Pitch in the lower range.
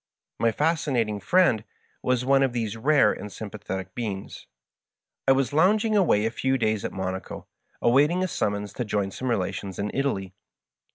Yes: low, 115 Hz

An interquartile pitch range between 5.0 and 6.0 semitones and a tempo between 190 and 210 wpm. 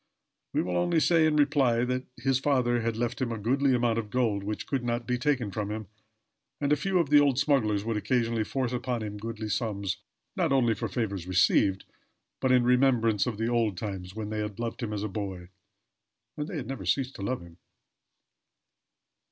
No: average, 3.9 semitones; average, 200 wpm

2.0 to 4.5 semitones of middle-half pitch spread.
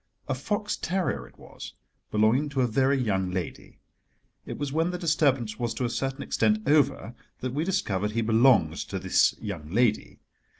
No: wide, 5.5 semitones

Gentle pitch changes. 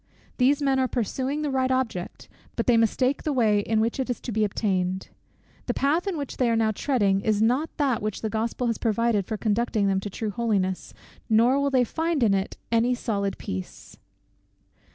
No: average, 3.8 semitones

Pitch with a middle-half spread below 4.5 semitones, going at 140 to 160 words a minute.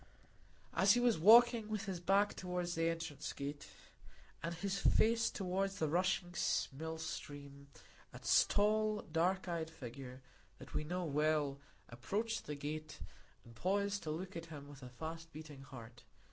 No: average, 5.1 semitones; average, 155 wpm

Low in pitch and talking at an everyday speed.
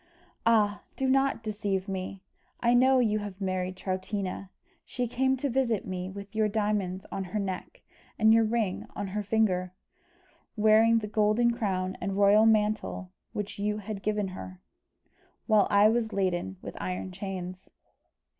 No: high, 205 Hz; average, 155 wpm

